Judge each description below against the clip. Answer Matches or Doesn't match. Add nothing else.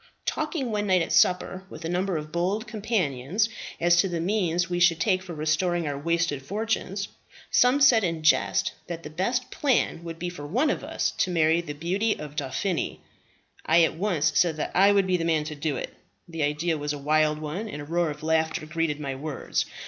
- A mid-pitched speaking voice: Matches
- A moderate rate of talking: Doesn't match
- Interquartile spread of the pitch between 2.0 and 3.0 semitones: Doesn't match